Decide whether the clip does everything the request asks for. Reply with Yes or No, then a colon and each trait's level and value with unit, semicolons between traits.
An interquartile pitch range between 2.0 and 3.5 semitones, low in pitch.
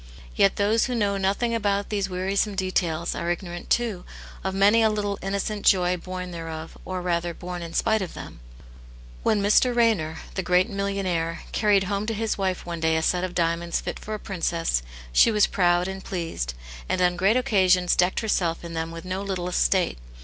No: average, 2.7 semitones; medium, 185 Hz